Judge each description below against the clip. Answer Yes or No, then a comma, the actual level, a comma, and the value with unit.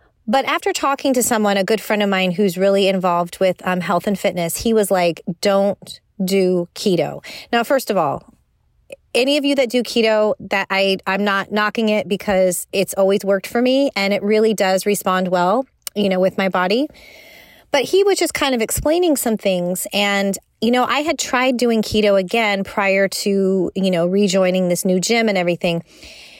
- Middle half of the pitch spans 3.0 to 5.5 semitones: Yes, average, 3.5 semitones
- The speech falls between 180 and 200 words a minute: Yes, average, 195 wpm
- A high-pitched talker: Yes, high, 200 Hz